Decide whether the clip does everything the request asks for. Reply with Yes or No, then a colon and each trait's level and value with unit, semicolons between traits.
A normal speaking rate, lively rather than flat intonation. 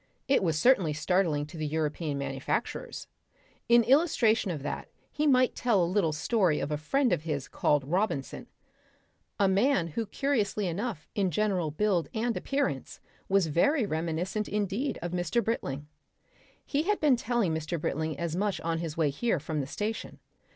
Yes: average, 165 wpm; wide, 6.4 semitones